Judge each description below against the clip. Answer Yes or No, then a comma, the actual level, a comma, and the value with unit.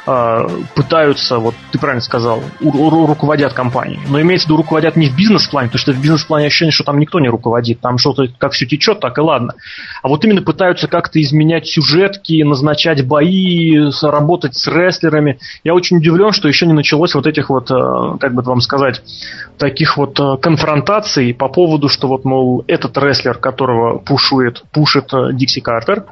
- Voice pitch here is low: No, medium, 150 Hz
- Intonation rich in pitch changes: No, average, 3.3 semitones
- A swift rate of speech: Yes, fast, 175 wpm